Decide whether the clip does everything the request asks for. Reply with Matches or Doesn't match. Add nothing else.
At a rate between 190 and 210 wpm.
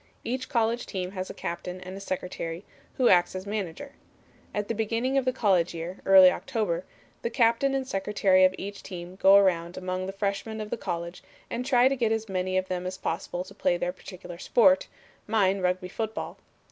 Matches